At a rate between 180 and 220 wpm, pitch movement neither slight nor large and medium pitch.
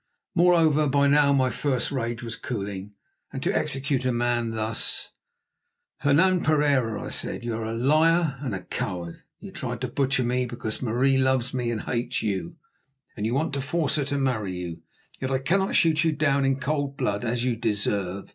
No: average, 190 wpm; average, 3.9 semitones; low, 130 Hz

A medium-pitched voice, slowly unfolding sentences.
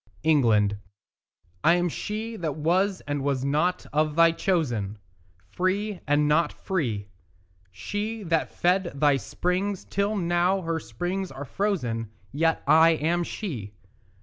Yes: medium, 165 Hz; slow, 130 wpm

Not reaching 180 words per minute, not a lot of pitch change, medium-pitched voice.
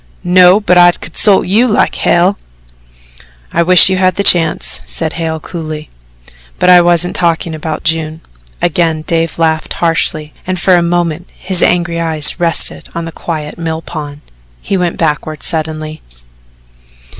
Yes: average, 150 wpm; narrow, 2.0 semitones; medium, 170 Hz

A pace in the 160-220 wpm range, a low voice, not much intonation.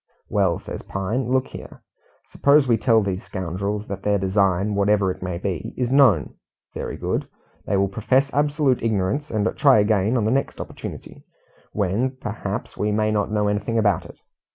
No: average, 175 wpm; low, 105 Hz; average, 3.9 semitones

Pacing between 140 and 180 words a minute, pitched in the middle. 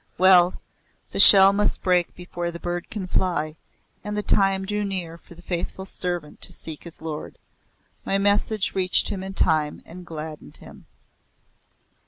Yes: average, 160 wpm; medium, 180 Hz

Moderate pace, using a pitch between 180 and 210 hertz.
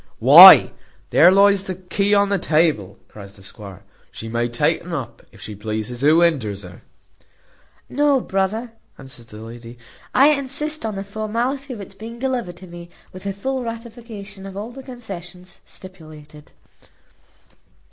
Yes: average, 155 wpm; medium, 185 Hz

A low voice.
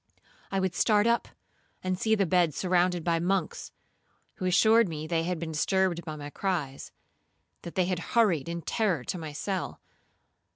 No: medium, 180 Hz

